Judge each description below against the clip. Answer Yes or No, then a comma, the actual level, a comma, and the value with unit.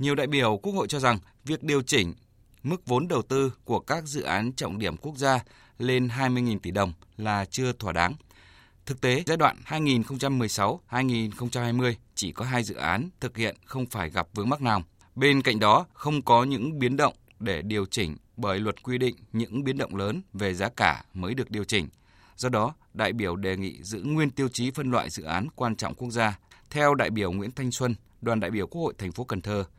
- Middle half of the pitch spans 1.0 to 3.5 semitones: No, average, 4.5 semitones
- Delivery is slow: No, average, 215 wpm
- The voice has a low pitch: Yes, low, 115 Hz